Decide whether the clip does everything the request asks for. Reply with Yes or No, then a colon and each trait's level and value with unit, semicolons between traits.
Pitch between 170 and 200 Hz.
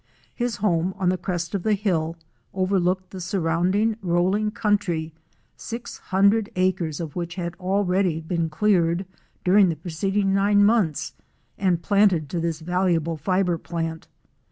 Yes: medium, 185 Hz